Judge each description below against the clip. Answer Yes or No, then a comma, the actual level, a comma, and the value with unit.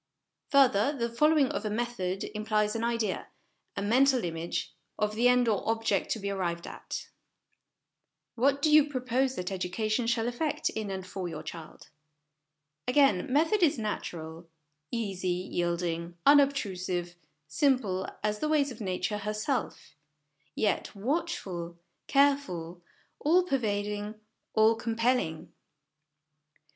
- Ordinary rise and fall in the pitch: No, wide, 5.9 semitones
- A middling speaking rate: No, slow, 125 wpm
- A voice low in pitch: No, high, 215 Hz